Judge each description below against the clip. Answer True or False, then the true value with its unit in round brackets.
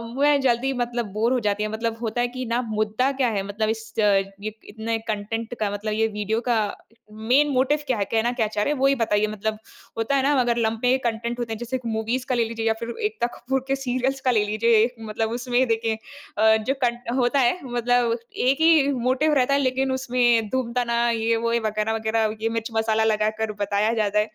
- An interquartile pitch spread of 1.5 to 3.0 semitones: True (2.4 semitones)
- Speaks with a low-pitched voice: False (230 Hz)